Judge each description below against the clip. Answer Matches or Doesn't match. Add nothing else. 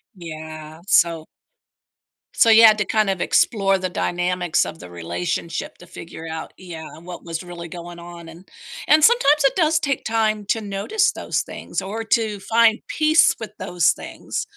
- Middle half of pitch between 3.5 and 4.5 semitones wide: Doesn't match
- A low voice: Doesn't match